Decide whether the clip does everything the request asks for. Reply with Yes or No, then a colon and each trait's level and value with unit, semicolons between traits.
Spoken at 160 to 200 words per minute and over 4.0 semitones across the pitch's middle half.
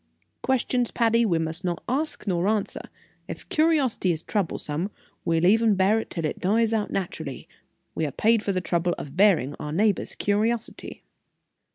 Yes: average, 165 wpm; average, 5.0 semitones